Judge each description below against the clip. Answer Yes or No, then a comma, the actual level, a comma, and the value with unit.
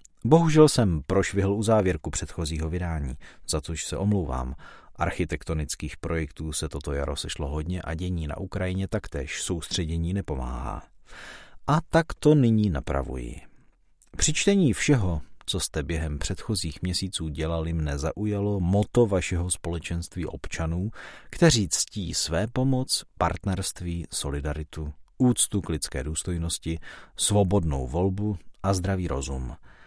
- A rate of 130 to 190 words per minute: No, average, 120 wpm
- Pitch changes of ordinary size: Yes, average, 4.5 semitones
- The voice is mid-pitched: No, very low, 85 Hz